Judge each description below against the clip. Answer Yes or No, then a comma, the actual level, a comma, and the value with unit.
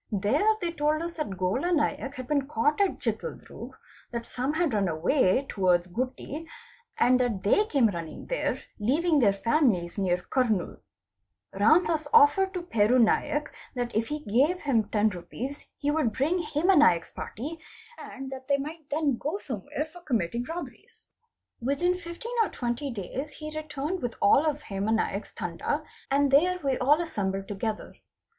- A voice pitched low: No, very high, 275 Hz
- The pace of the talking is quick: No, average, 165 wpm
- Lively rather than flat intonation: Yes, wide, 6.1 semitones